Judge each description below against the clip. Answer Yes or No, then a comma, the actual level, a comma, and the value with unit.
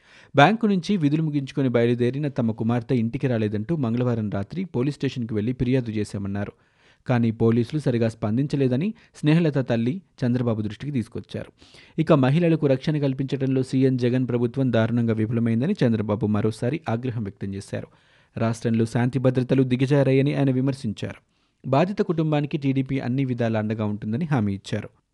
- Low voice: Yes, low, 125 Hz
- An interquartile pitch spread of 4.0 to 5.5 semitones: No, average, 3.5 semitones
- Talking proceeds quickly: Yes, fast, 130 wpm